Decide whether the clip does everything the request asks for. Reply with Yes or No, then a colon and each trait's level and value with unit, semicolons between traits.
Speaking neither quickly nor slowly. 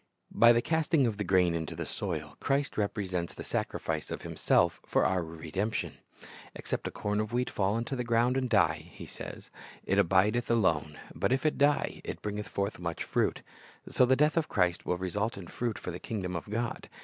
No: fast, 210 wpm